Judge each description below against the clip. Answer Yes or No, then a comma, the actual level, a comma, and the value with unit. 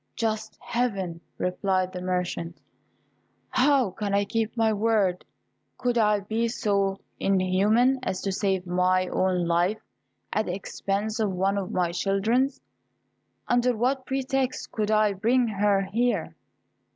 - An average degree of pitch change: Yes, average, 3.7 semitones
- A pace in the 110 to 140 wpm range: Yes, slow, 135 wpm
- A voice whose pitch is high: Yes, high, 205 Hz